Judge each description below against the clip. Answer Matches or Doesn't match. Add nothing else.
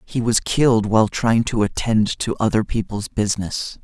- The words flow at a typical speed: Matches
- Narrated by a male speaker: Matches